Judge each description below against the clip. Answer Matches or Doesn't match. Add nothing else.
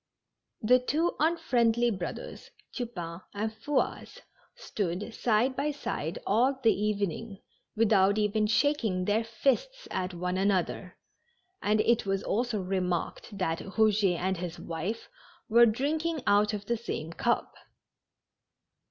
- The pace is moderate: Doesn't match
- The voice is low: Doesn't match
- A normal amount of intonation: Matches